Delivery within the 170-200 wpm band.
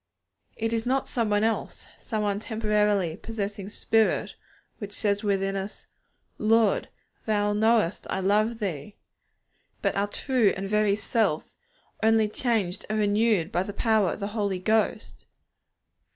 No: average, 140 wpm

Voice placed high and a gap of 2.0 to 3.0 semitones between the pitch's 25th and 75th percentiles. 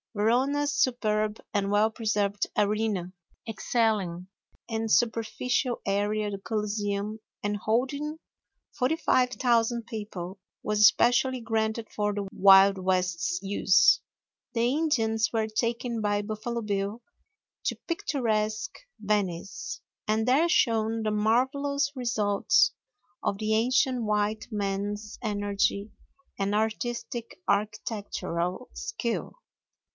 Yes: high, 215 Hz; average, 2.7 semitones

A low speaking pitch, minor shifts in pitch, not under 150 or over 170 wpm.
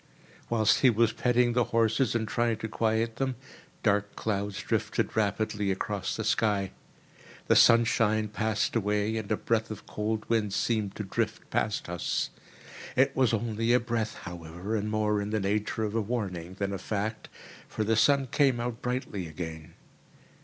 Yes: low, 110 Hz; narrow, 2.2 semitones; average, 165 wpm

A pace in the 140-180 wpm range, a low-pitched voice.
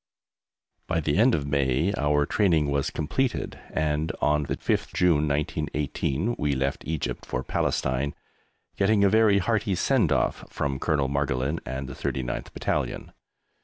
Yes: average, 145 wpm; very low, 75 Hz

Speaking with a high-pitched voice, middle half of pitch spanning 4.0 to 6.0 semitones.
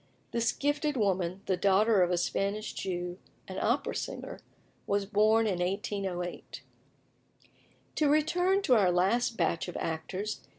Yes: high, 200 Hz; average, 4.3 semitones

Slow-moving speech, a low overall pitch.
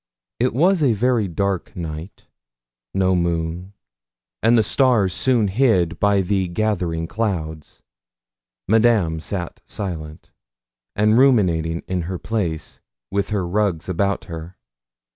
Yes: slow, 120 wpm; very low, 95 Hz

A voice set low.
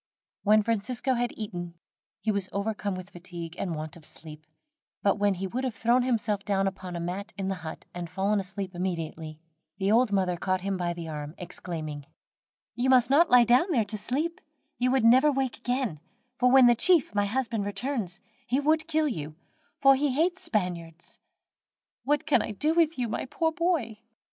No: high, 210 Hz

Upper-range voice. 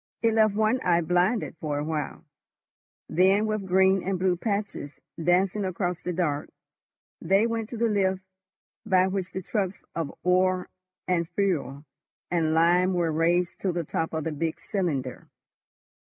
No: medium, 180 Hz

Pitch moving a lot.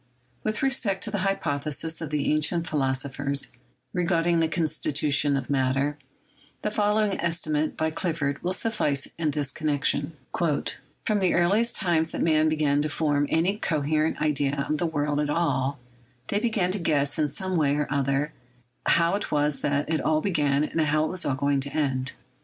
No: average, 3.2 semitones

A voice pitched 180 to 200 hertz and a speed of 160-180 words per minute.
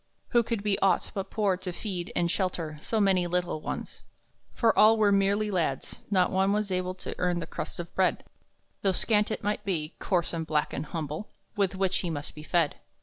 No: medium, 185 Hz; fast, 205 wpm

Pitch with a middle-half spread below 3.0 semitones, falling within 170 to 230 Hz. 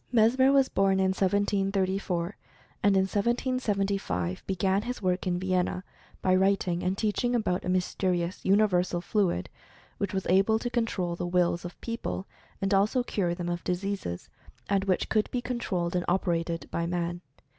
Yes: narrow, 2.4 semitones; high, 190 Hz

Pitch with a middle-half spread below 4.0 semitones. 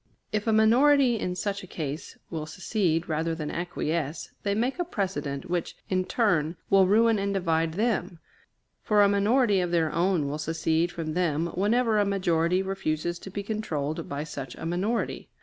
No: average, 4.3 semitones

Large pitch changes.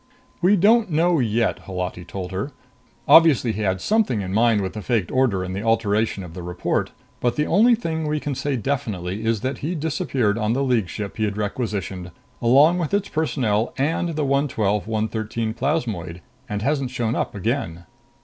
Yes: wide, 6.1 semitones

